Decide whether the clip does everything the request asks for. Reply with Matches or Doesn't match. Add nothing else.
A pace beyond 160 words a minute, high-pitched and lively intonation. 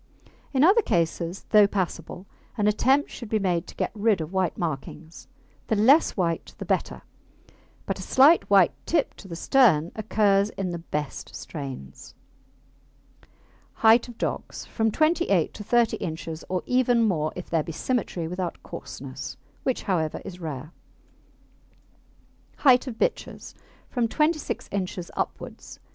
Doesn't match